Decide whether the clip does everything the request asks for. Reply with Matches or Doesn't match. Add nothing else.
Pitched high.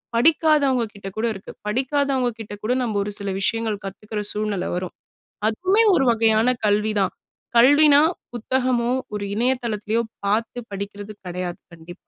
Matches